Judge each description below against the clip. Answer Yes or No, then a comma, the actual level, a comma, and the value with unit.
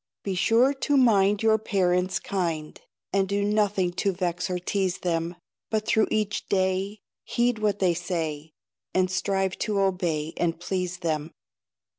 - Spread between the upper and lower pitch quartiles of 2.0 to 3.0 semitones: Yes, average, 2.7 semitones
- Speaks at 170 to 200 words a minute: No, average, 150 wpm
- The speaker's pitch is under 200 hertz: Yes, high, 190 Hz